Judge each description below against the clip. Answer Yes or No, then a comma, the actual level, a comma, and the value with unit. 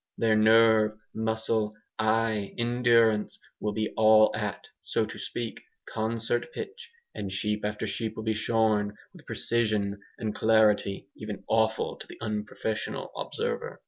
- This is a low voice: Yes, low, 110 Hz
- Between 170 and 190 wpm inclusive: No, average, 140 wpm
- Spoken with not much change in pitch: Yes, narrow, 1.1 semitones